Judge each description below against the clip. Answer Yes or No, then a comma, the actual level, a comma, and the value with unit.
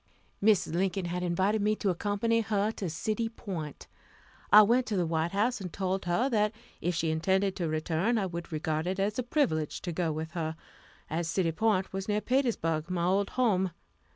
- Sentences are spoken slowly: No, average, 195 wpm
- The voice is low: No, high, 190 Hz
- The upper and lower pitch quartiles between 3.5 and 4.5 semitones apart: Yes, average, 4.1 semitones